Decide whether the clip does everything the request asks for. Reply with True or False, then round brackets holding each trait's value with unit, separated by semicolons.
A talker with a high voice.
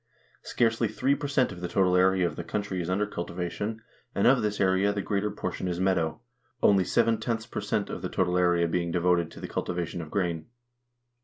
False (95 Hz)